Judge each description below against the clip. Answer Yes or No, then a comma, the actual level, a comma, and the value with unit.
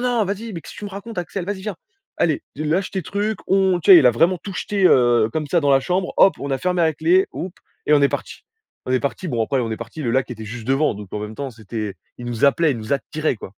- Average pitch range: No, wide, 7.5 semitones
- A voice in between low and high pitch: Yes, medium, 155 Hz